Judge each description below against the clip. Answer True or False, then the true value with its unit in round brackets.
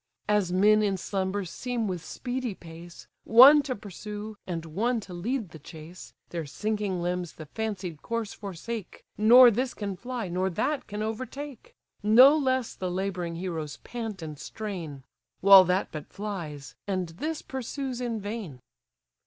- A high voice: True (200 Hz)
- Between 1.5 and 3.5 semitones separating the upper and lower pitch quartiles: False (4.9 semitones)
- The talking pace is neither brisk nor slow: True (155 wpm)